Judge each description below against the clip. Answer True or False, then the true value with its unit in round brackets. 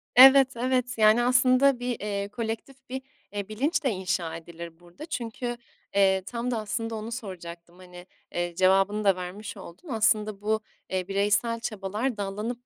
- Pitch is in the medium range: False (215 Hz)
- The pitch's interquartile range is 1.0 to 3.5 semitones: False (4.3 semitones)